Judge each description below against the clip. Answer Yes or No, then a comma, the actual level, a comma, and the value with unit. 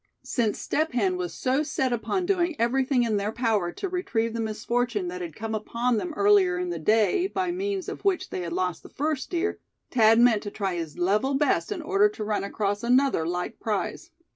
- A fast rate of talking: Yes, fast, 210 wpm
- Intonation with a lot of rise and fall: Yes, wide, 6.9 semitones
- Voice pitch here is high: Yes, high, 230 Hz